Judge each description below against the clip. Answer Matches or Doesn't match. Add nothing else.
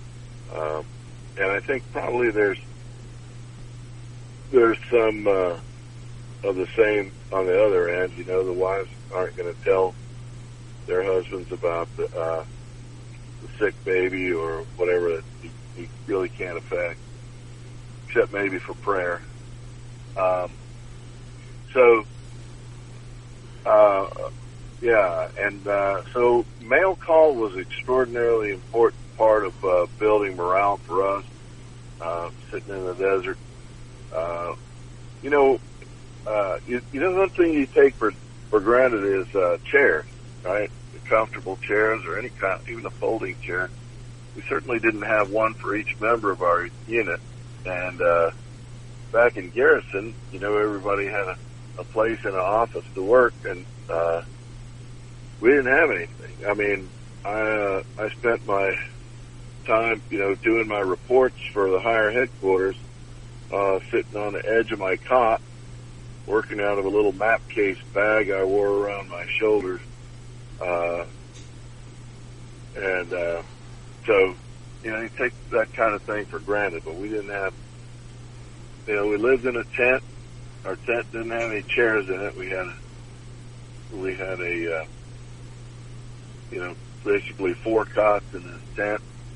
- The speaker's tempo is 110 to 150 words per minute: Matches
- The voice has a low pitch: Matches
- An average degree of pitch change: Doesn't match